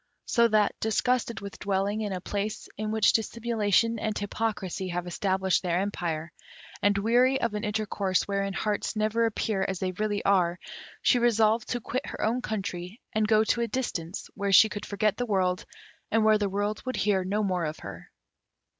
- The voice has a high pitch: Yes, high, 210 Hz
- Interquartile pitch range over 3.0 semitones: No, narrow, 2.4 semitones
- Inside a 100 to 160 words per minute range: No, average, 185 wpm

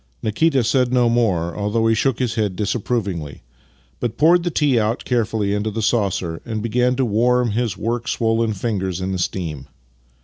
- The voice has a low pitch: Yes, low, 115 Hz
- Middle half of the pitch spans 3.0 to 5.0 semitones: Yes, average, 3.3 semitones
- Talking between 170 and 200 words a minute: Yes, average, 175 wpm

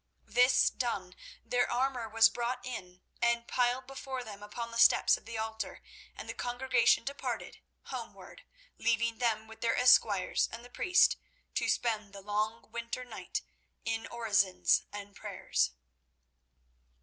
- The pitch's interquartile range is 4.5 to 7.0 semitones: No, narrow, 2.5 semitones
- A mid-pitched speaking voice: No, high, 230 Hz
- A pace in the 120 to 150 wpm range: Yes, average, 140 wpm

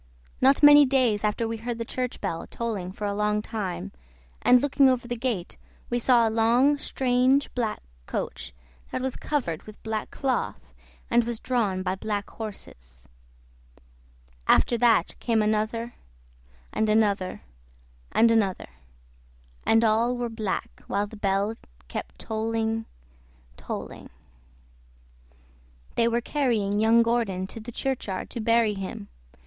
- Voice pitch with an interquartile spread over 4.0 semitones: No, average, 2.8 semitones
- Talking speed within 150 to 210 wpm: No, slow, 135 wpm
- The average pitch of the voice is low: No, high, 225 Hz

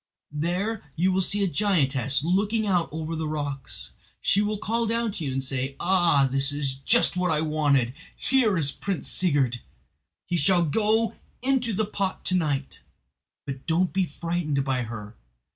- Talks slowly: No, average, 170 wpm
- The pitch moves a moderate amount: No, wide, 6.1 semitones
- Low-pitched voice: No, medium, 165 Hz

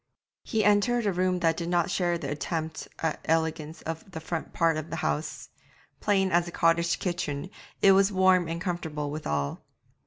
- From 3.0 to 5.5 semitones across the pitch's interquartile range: No, narrow, 2.5 semitones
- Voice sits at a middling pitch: Yes, medium, 170 Hz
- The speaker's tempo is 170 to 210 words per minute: Yes, average, 180 wpm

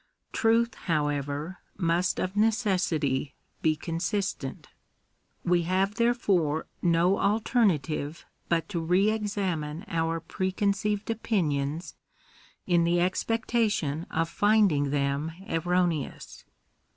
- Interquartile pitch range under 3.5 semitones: No, average, 4.6 semitones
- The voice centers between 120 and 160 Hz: No, medium, 175 Hz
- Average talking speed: No, slow, 100 wpm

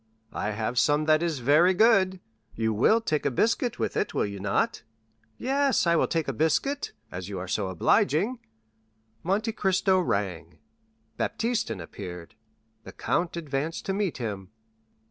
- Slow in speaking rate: No, average, 155 wpm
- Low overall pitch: No, medium, 155 Hz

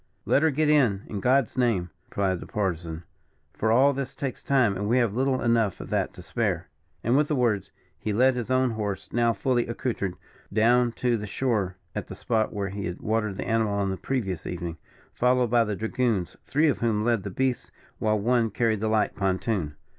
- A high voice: No, low, 110 Hz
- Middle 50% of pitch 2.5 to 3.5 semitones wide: No, average, 3.9 semitones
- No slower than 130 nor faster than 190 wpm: No, fast, 205 wpm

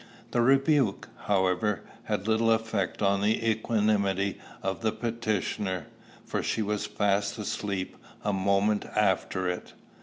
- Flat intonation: Yes, narrow, 2.2 semitones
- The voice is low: Yes, low, 105 Hz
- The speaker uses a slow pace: Yes, slow, 125 wpm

